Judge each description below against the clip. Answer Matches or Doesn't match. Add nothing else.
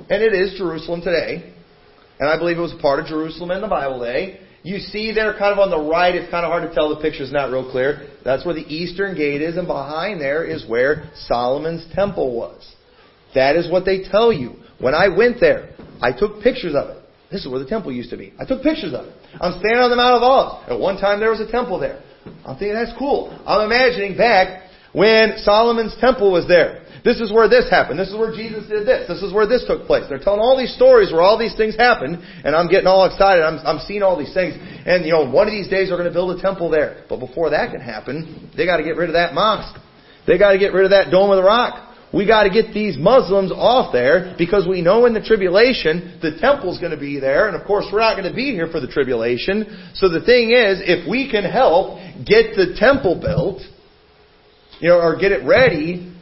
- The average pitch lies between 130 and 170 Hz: Doesn't match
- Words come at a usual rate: Doesn't match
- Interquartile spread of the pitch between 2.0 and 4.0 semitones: Doesn't match